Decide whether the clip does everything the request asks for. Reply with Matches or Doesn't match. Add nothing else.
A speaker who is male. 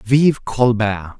Matches